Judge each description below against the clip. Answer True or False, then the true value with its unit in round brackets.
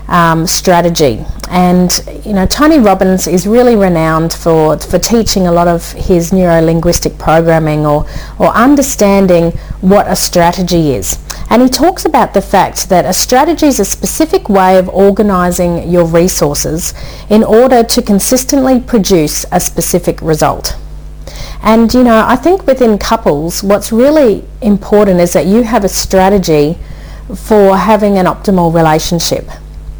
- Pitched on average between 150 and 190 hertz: True (185 Hz)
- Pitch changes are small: False (4.7 semitones)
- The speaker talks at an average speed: True (145 wpm)